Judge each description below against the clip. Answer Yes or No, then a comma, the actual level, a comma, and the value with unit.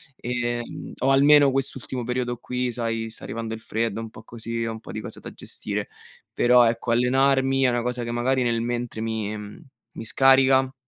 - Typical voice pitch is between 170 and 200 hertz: No, low, 120 Hz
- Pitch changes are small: Yes, narrow, 2.3 semitones